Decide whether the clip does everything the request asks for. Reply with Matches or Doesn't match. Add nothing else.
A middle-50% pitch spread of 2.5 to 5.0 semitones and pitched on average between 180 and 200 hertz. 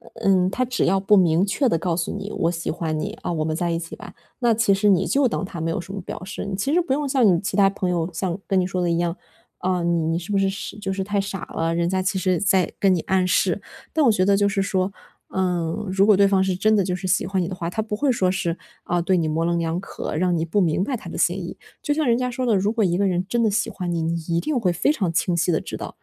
Matches